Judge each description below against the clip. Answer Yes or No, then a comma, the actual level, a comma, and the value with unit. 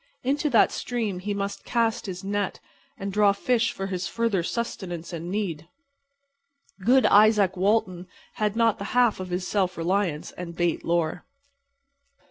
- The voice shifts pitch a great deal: No, average, 3.7 semitones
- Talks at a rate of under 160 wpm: Yes, average, 150 wpm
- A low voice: No, high, 200 Hz